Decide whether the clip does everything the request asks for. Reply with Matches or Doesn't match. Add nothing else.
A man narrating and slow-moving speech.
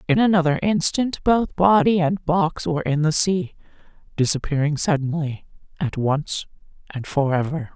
Doesn't match